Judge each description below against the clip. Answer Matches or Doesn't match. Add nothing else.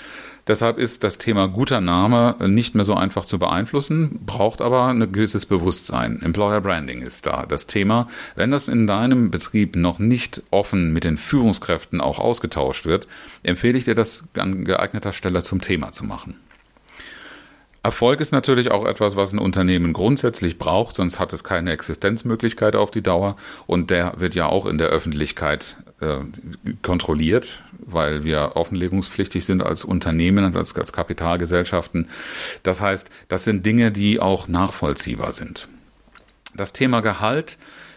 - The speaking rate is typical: Matches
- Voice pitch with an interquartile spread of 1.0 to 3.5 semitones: Doesn't match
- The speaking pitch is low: Matches